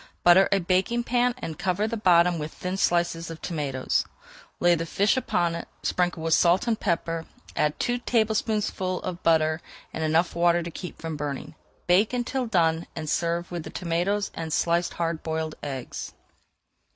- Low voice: No, medium, 175 Hz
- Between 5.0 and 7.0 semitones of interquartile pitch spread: No, average, 2.9 semitones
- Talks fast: No, average, 170 wpm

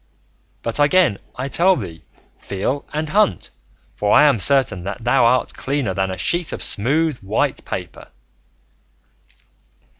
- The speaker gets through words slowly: Yes, slow, 130 wpm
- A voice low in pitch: Yes, low, 130 Hz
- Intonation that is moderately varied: No, wide, 7.0 semitones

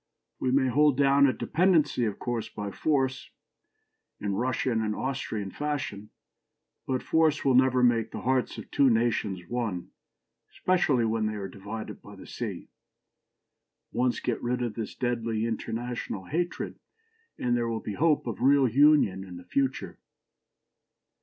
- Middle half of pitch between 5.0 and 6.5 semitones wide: No, average, 3.9 semitones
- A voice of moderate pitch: No, low, 120 Hz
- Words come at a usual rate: Yes, average, 150 wpm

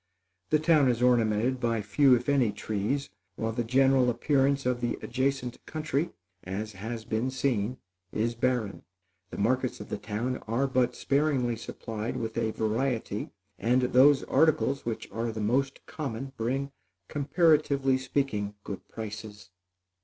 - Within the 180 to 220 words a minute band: No, average, 145 wpm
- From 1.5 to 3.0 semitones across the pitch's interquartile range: No, average, 3.5 semitones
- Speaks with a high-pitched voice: No, low, 125 Hz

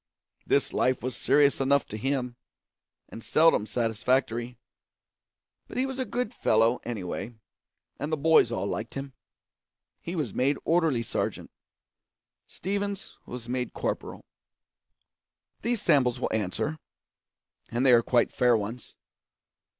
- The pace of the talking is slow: Yes, slow, 125 wpm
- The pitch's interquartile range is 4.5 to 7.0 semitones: Yes, average, 4.9 semitones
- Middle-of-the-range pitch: No, low, 125 Hz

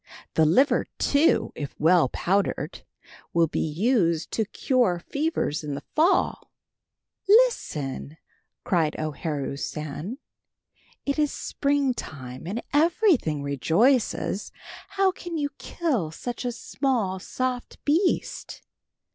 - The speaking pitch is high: Yes, high, 215 Hz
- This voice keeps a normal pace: No, slow, 110 wpm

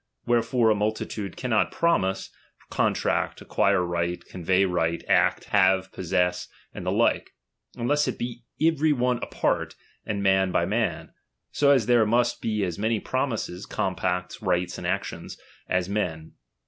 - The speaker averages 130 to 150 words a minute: Yes, average, 145 wpm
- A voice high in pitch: No, low, 100 Hz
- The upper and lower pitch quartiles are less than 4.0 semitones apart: No, average, 4.8 semitones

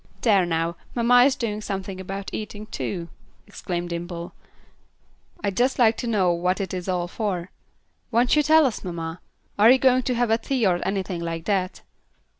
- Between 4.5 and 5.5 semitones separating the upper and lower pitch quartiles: Yes, average, 4.9 semitones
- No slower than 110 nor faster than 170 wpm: No, average, 180 wpm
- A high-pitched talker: Yes, high, 195 Hz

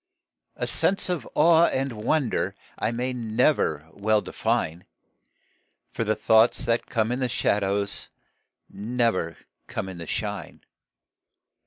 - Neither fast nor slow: No, slow, 130 wpm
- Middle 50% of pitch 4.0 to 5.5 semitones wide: No, average, 3.6 semitones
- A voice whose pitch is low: Yes, low, 115 Hz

